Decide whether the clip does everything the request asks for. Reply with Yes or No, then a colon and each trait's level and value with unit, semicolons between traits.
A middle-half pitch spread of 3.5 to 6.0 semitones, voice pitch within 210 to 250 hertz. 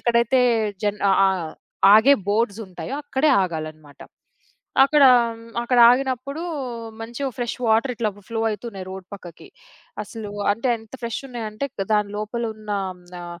Yes: average, 4.0 semitones; high, 220 Hz